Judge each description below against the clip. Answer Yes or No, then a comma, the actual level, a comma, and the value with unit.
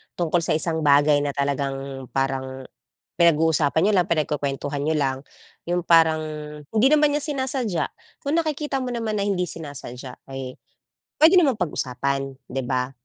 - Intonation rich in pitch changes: Yes, wide, 7.0 semitones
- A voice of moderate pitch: Yes, medium, 155 Hz